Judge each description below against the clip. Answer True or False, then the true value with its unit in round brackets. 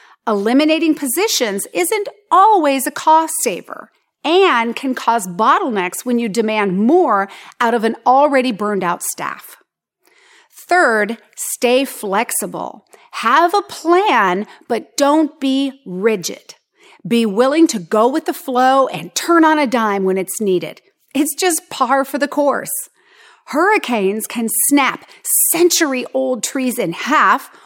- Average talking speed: False (130 wpm)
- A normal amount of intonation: False (6.8 semitones)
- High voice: True (270 Hz)